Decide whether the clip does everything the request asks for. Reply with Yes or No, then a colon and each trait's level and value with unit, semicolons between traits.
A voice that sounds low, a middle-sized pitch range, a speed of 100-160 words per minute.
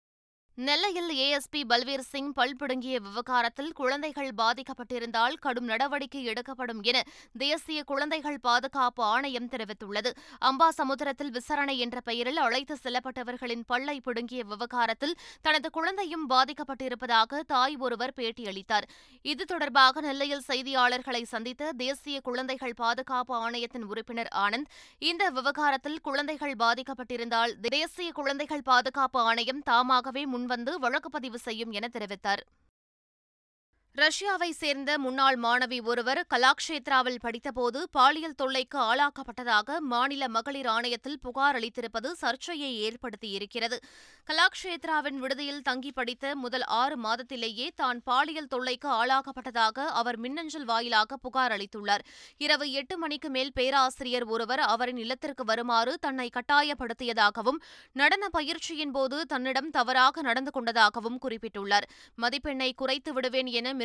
No: very high, 260 Hz; average, 3.1 semitones; average, 110 wpm